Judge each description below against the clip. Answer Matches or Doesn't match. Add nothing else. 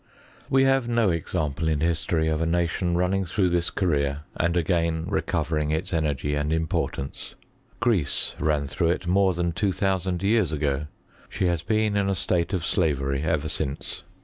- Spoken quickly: Doesn't match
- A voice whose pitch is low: Matches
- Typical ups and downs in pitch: Matches